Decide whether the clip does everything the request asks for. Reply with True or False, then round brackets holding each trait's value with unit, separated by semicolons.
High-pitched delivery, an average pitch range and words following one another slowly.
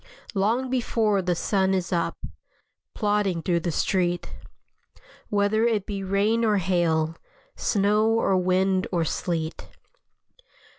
True (195 Hz; 3.1 semitones; 115 wpm)